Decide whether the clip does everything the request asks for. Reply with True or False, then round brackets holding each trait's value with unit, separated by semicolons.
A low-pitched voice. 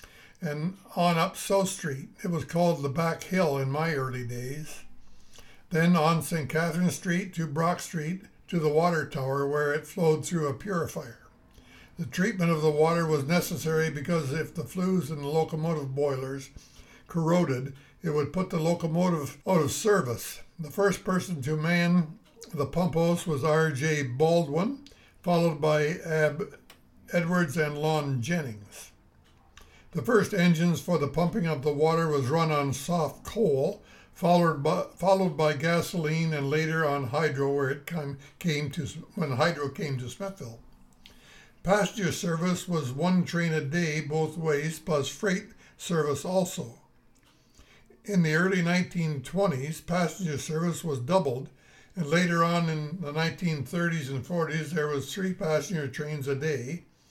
False (160 Hz)